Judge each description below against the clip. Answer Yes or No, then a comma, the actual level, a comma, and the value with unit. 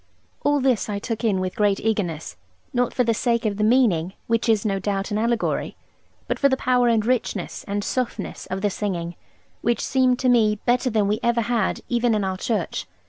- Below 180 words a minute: No, fast, 205 wpm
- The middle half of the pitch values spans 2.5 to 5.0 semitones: Yes, average, 3.3 semitones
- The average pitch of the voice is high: Yes, high, 220 Hz